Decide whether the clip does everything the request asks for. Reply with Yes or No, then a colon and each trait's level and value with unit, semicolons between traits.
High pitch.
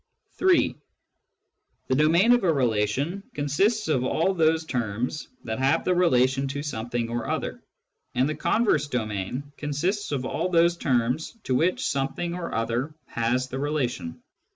No: medium, 140 Hz